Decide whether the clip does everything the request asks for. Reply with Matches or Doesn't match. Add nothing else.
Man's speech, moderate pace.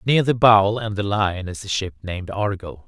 Doesn't match